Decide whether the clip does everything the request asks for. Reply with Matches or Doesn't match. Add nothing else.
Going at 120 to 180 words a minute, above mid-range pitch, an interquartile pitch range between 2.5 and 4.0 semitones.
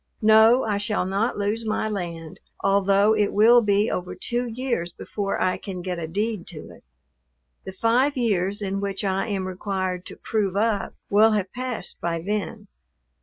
Matches